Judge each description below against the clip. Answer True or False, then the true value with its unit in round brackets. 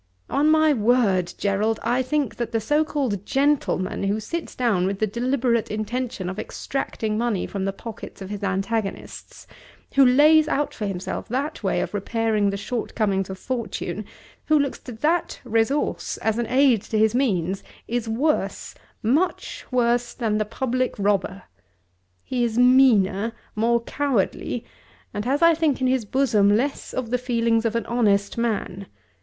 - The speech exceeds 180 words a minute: False (160 wpm)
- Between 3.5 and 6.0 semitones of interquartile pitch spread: True (3.9 semitones)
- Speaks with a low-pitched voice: False (230 Hz)